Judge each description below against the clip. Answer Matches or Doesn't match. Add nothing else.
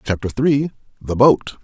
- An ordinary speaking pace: Matches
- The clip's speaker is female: Doesn't match